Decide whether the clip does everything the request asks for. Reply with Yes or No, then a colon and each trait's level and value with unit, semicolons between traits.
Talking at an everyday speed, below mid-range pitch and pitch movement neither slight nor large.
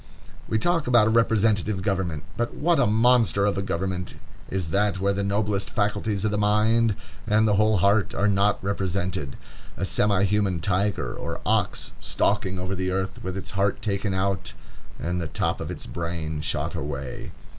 No: average, 175 wpm; low, 100 Hz; narrow, 2.3 semitones